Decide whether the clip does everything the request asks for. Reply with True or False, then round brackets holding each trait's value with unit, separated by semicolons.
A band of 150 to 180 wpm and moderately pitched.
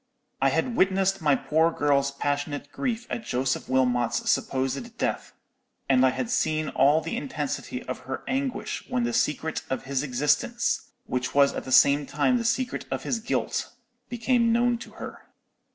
True (170 wpm; 150 Hz)